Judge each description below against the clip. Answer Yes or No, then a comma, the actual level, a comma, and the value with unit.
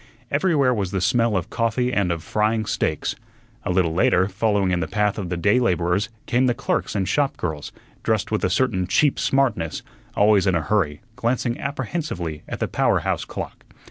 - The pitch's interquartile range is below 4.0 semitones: No, average, 5.2 semitones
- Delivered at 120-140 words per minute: No, average, 190 wpm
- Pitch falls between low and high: No, low, 105 Hz